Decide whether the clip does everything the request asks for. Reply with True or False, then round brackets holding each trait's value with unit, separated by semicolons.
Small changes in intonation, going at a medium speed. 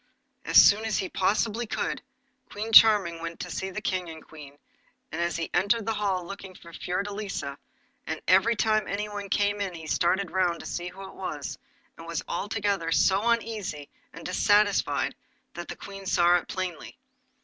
False (3.2 semitones; 180 wpm)